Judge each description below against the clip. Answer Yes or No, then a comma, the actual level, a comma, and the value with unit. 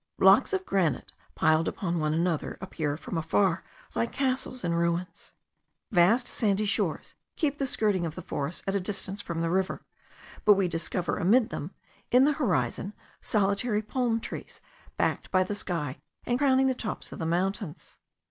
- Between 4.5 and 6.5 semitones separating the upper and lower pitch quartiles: Yes, average, 5.2 semitones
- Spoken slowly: No, average, 165 wpm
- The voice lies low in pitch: No, high, 195 Hz